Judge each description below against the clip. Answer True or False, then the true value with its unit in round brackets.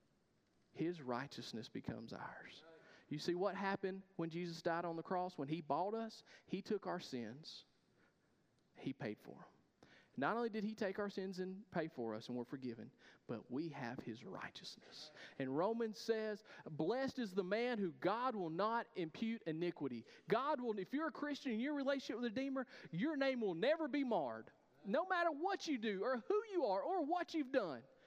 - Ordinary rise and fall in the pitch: False (7.5 semitones)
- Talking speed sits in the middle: True (195 wpm)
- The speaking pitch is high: True (205 Hz)